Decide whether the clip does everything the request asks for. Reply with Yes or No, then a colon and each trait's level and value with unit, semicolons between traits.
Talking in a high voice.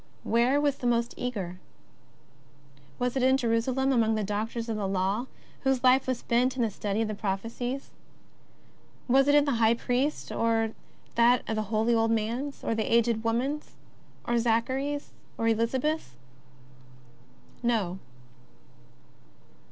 Yes: high, 235 Hz